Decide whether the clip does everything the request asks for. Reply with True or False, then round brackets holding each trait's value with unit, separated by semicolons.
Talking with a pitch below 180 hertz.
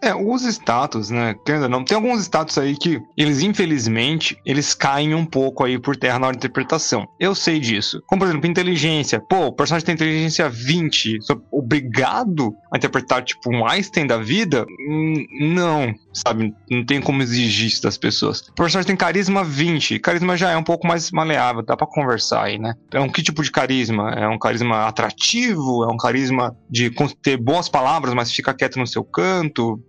True (140 Hz)